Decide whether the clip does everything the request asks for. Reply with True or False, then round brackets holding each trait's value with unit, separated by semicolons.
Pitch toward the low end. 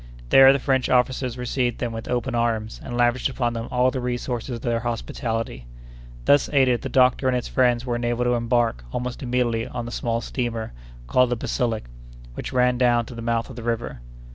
True (120 Hz)